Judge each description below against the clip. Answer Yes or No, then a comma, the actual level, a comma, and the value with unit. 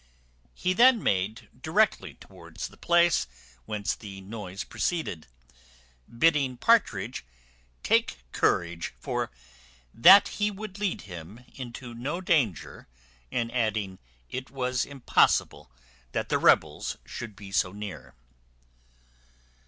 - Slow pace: Yes, slow, 105 wpm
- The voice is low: Yes, low, 120 Hz